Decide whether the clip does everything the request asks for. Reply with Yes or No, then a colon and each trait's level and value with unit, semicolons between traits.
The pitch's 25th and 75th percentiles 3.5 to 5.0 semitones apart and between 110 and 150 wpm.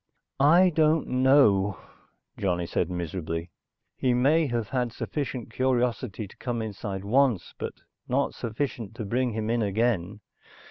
Yes: average, 4.7 semitones; slow, 135 wpm